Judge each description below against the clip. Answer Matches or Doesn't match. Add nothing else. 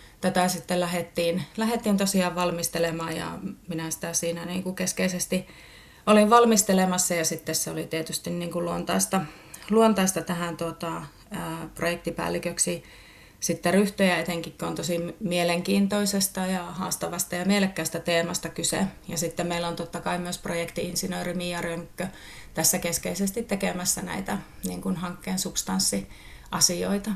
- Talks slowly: Doesn't match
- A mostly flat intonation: Matches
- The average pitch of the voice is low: Doesn't match